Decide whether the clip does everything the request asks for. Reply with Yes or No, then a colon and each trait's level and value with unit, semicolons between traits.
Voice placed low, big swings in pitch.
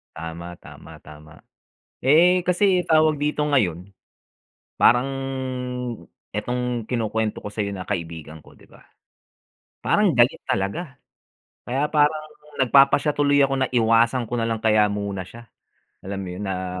Yes: low, 115 Hz; wide, 6.8 semitones